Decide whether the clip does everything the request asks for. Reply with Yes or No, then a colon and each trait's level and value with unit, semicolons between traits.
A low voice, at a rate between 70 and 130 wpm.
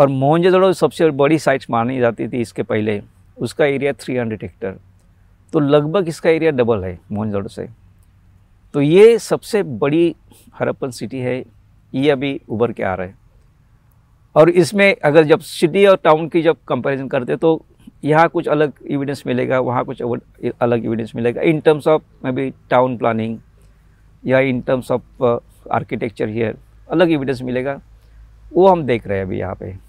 No: low, 130 Hz; average, 170 wpm